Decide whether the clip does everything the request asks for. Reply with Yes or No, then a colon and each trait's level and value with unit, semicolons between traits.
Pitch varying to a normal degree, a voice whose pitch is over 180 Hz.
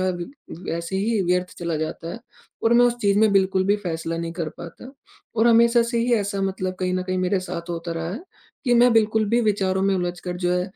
Yes: average, 3.8 semitones; high, 190 Hz